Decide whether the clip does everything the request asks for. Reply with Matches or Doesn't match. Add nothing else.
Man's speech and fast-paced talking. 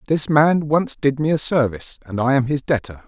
Matches